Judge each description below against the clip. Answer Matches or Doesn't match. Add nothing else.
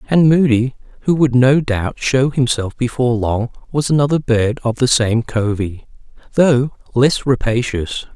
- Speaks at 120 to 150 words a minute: Matches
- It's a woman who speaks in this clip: Doesn't match